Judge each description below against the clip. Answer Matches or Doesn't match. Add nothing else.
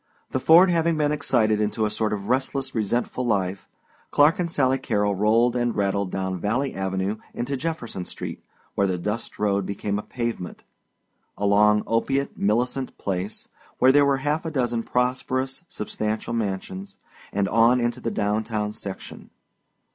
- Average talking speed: Matches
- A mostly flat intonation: Doesn't match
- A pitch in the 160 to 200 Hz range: Doesn't match